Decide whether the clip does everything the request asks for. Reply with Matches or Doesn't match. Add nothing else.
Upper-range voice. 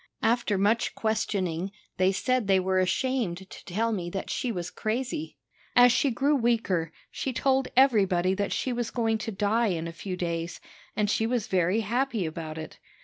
Matches